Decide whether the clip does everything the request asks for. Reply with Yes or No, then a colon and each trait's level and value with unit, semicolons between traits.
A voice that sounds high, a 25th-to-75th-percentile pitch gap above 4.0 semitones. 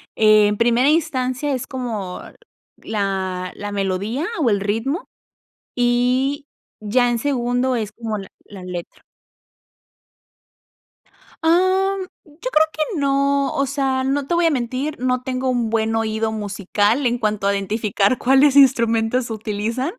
Yes: high, 245 Hz; average, 4.4 semitones